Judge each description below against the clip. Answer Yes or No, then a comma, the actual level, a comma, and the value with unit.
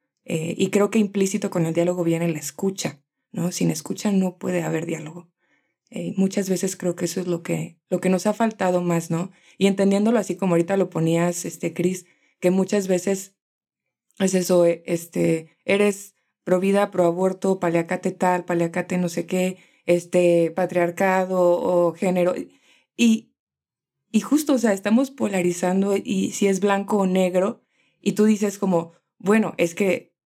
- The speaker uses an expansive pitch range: No, narrow, 2.4 semitones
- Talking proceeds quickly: No, average, 175 wpm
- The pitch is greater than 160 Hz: Yes, medium, 185 Hz